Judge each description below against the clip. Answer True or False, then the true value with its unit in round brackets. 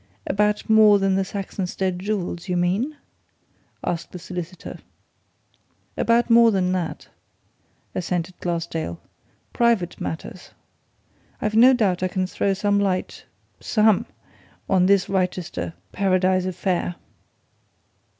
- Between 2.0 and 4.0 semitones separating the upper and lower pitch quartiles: True (2.5 semitones)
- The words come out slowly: True (110 wpm)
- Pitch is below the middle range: False (185 Hz)